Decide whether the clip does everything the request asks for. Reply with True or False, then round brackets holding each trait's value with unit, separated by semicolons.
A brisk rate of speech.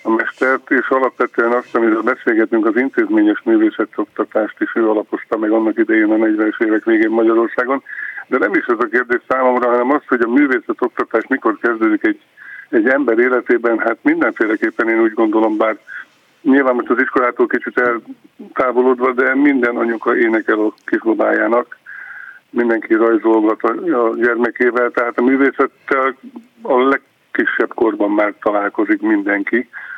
False (145 wpm)